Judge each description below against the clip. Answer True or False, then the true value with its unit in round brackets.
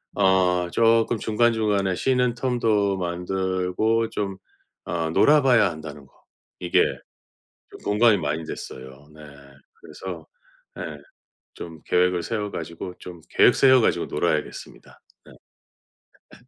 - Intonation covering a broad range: False (4.7 semitones)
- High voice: False (95 Hz)